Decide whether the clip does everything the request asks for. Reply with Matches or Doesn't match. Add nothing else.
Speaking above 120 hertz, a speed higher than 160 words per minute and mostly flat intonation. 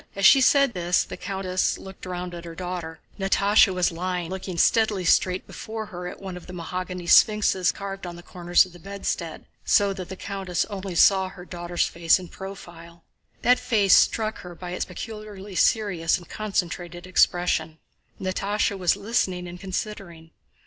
Matches